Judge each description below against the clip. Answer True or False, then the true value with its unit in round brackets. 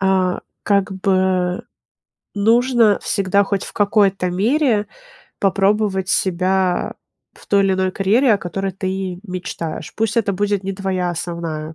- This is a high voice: True (195 Hz)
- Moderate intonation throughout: False (2.0 semitones)